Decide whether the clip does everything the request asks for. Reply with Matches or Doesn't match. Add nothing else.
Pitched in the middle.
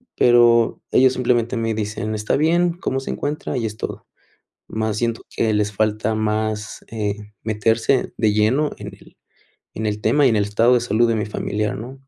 Doesn't match